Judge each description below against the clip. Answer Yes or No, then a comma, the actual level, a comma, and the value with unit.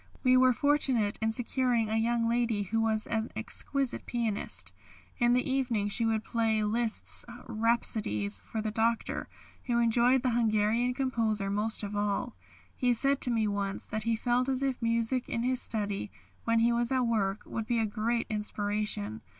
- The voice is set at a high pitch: Yes, high, 230 Hz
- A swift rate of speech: No, average, 175 wpm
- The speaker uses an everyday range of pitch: No, narrow, 2.2 semitones